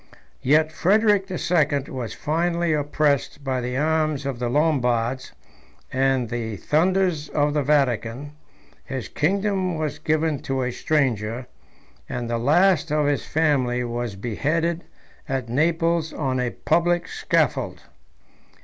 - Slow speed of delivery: Yes, slow, 130 wpm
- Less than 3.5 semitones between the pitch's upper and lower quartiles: No, average, 4.4 semitones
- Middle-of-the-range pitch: Yes, medium, 145 Hz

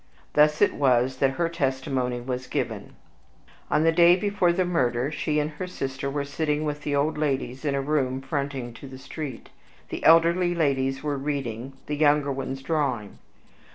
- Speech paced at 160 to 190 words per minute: Yes, average, 175 wpm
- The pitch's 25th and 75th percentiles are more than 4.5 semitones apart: No, narrow, 2.6 semitones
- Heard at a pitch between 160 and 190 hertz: No, medium, 140 Hz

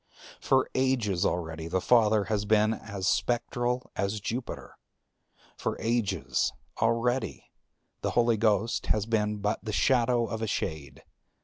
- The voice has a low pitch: Yes, low, 110 Hz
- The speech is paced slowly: Yes, slow, 130 wpm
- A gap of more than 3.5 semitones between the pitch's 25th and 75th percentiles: No, average, 2.8 semitones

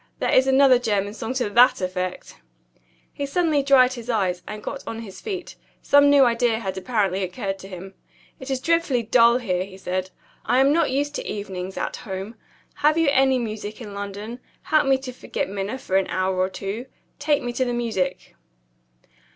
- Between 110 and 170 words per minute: No, average, 190 wpm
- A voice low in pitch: No, high, 230 Hz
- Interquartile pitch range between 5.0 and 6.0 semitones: Yes, wide, 5.5 semitones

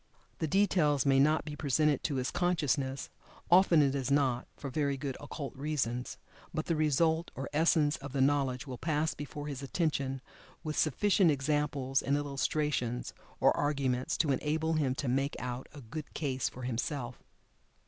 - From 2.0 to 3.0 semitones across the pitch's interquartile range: Yes, narrow, 2.5 semitones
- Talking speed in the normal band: Yes, average, 165 wpm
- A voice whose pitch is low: No, medium, 145 Hz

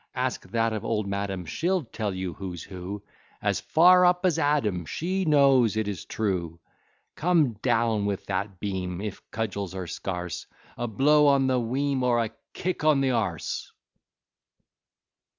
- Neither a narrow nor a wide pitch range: No, wide, 6.5 semitones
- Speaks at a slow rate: No, average, 160 wpm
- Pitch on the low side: Yes, low, 110 Hz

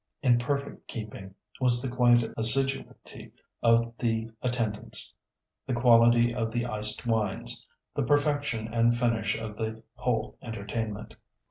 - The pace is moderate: No, slow, 125 wpm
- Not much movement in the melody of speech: Yes, narrow, 1.7 semitones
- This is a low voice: Yes, low, 115 Hz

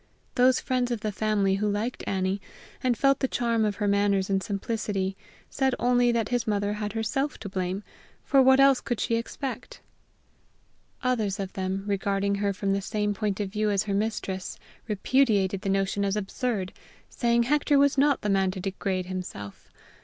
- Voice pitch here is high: Yes, high, 210 Hz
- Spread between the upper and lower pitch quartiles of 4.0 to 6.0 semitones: No, average, 3.6 semitones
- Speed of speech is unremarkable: Yes, average, 180 wpm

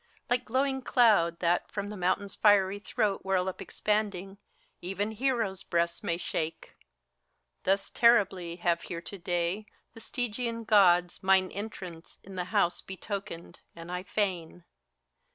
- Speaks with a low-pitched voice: No, high, 195 Hz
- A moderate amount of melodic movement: Yes, average, 3.2 semitones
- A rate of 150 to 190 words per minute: No, slow, 135 wpm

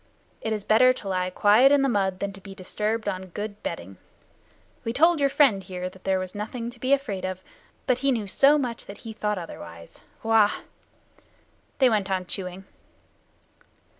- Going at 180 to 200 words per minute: Yes, average, 185 wpm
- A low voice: No, high, 210 Hz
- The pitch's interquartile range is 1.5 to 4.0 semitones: No, average, 4.4 semitones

